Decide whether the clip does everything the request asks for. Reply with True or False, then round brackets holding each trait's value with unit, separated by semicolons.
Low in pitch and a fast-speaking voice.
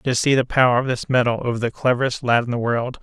True (125 Hz; 275 wpm)